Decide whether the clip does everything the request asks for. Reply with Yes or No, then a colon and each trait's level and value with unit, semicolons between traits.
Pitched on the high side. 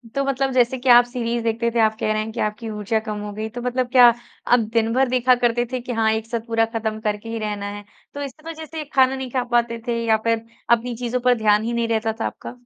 Yes: high, 235 Hz